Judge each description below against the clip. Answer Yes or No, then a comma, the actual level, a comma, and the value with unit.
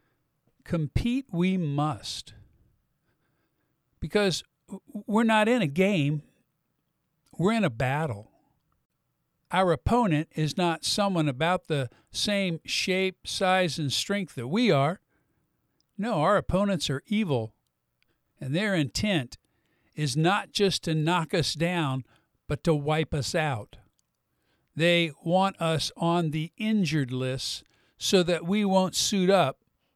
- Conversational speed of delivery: No, slow, 120 wpm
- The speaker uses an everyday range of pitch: Yes, average, 4.9 semitones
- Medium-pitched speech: Yes, medium, 165 Hz